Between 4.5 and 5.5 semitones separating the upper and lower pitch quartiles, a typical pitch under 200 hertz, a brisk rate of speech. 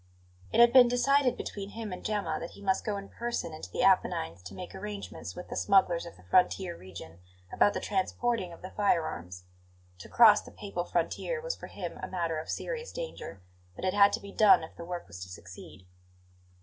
Yes: average, 4.9 semitones; high, 190 Hz; fast, 210 wpm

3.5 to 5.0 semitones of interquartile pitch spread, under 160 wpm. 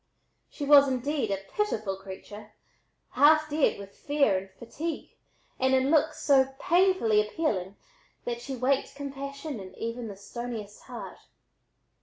No: wide, 5.5 semitones; slow, 135 wpm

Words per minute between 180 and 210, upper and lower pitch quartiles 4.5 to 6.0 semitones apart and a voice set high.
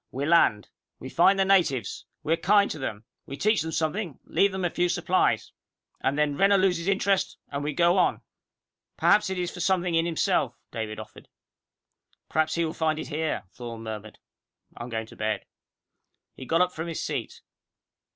No: average, 190 wpm; average, 5.2 semitones; medium, 165 Hz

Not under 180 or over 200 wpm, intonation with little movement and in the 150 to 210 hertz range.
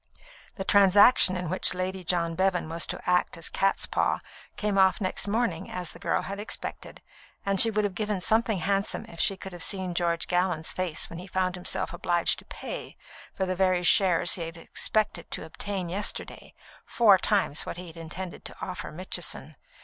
Yes: average, 190 wpm; narrow, 2.3 semitones; medium, 185 Hz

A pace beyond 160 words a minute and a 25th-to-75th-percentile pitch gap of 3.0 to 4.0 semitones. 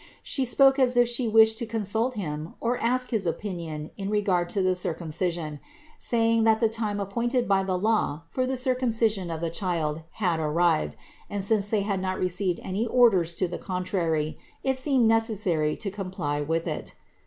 No: average, 180 wpm; average, 4.9 semitones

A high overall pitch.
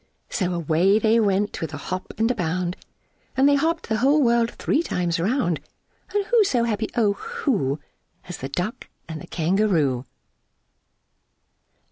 Yes: high, 205 Hz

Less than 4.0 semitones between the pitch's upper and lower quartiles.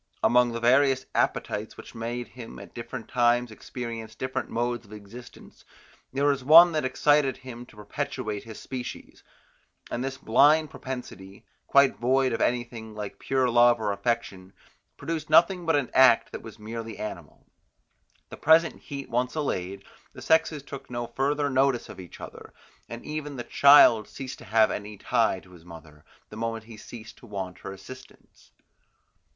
Yes: average, 3.5 semitones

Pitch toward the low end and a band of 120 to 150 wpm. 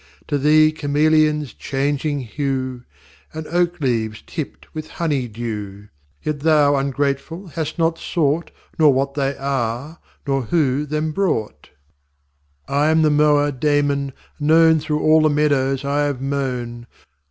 No: medium, 145 Hz; average, 140 wpm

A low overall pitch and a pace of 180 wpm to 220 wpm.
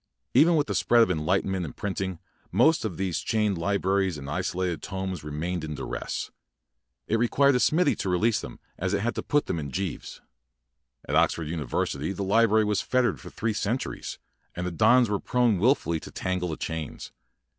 Yes: very low, 95 Hz; average, 200 wpm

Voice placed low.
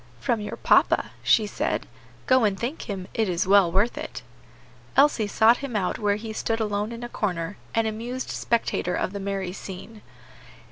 No: high, 210 Hz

